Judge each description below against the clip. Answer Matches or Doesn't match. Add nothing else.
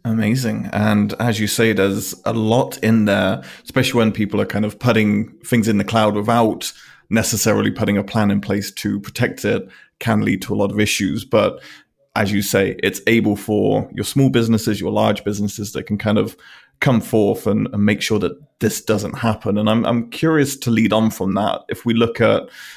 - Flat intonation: Matches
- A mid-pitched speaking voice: Doesn't match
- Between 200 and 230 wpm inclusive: Matches